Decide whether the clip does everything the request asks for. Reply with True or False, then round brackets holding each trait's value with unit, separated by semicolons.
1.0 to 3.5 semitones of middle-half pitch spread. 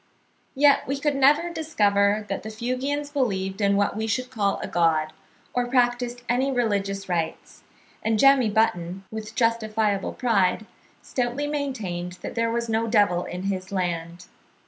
False (4.3 semitones)